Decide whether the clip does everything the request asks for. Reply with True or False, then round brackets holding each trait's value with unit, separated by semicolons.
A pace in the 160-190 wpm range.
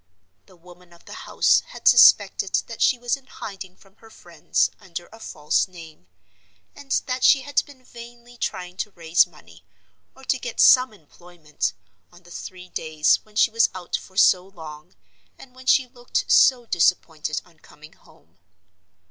True (170 wpm)